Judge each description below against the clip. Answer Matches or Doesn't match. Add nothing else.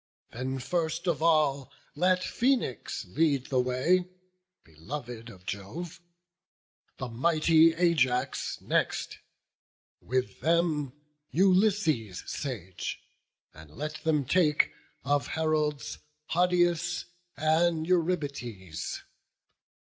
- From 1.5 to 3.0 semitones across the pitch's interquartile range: Doesn't match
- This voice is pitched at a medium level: Matches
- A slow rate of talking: Matches